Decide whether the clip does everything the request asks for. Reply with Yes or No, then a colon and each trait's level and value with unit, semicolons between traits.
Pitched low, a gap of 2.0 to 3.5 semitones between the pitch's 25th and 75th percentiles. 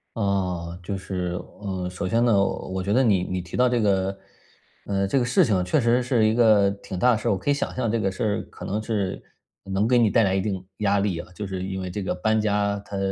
Yes: low, 100 Hz; average, 2.8 semitones